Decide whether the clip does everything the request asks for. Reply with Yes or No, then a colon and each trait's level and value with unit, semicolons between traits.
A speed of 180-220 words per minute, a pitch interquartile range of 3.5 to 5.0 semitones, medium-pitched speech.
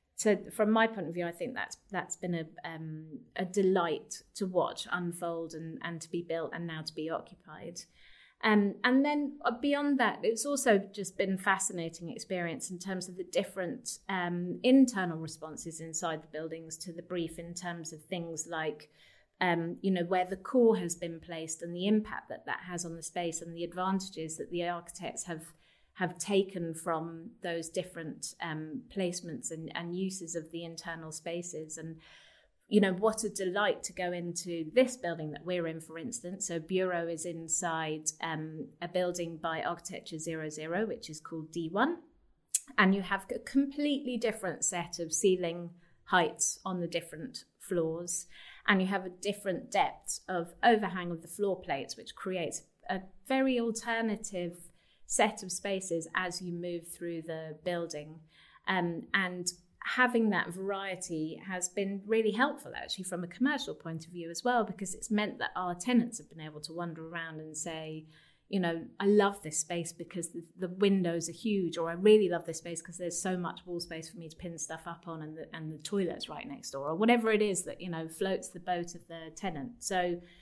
No: average, 190 wpm; average, 2.9 semitones; medium, 175 Hz